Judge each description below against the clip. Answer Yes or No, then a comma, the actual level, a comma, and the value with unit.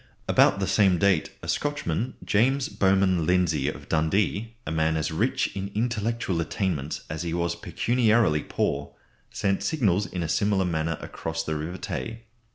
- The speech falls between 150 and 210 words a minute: Yes, average, 160 wpm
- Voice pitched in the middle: No, very low, 95 Hz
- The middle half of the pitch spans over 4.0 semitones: Yes, average, 4.6 semitones